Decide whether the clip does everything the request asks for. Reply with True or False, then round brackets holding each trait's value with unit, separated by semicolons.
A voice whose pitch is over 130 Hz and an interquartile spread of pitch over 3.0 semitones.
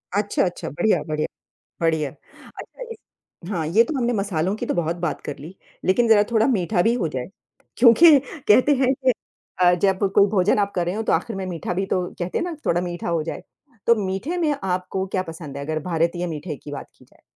True (185 Hz; 4.5 semitones)